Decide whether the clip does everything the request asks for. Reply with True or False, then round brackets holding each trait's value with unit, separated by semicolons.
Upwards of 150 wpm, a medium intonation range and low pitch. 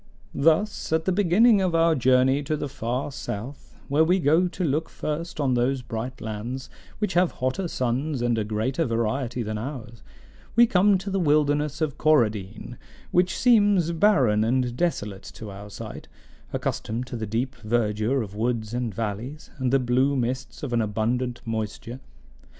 False (165 wpm; 5.7 semitones; 130 Hz)